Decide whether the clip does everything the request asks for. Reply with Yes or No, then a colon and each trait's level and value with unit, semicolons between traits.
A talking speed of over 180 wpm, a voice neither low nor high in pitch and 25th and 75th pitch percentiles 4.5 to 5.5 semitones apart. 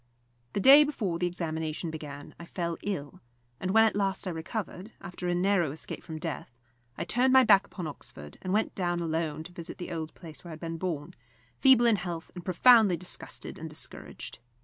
No: average, 200 wpm; medium, 175 Hz; average, 3.6 semitones